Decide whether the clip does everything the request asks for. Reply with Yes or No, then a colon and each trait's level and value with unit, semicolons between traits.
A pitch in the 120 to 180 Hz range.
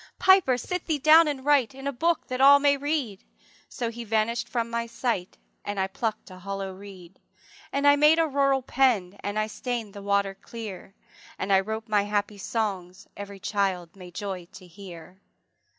No: high, 215 Hz